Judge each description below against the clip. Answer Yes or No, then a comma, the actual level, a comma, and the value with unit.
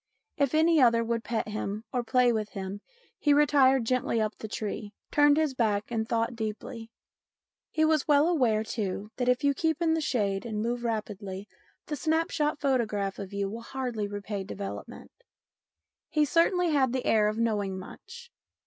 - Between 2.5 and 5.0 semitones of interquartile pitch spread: No, wide, 5.4 semitones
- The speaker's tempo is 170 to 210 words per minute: Yes, average, 175 wpm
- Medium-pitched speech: No, high, 230 Hz